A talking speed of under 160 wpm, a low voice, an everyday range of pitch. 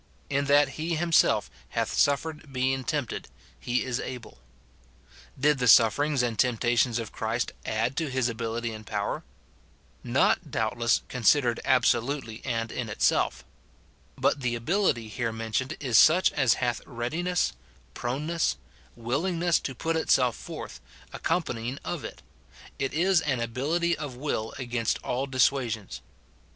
Yes: average, 140 wpm; low, 125 Hz; average, 4.0 semitones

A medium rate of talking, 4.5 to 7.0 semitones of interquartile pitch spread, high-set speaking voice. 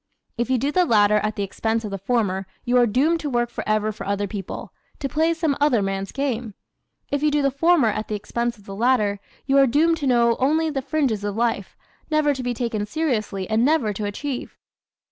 No: fast, 220 wpm; average, 5.2 semitones; high, 240 Hz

